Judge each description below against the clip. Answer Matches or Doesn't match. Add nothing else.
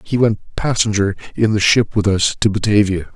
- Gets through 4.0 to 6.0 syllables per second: Matches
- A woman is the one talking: Doesn't match